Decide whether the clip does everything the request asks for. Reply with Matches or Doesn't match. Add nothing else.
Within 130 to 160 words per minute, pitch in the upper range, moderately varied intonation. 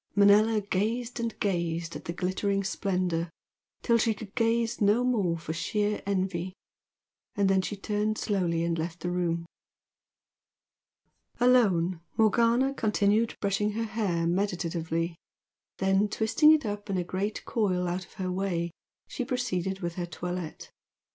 Matches